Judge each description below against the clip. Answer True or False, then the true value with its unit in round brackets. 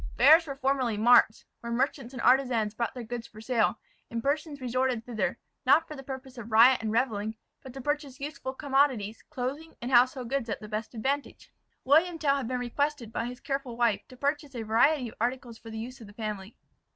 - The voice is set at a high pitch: True (250 Hz)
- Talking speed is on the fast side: True (210 wpm)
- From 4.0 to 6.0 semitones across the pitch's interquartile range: False (3.3 semitones)